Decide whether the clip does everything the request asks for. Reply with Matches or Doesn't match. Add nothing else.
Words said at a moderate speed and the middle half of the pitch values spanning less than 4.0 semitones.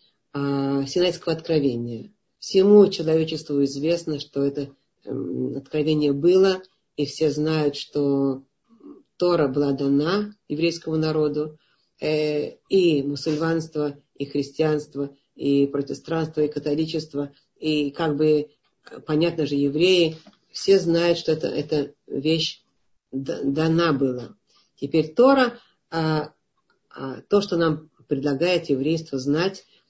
Doesn't match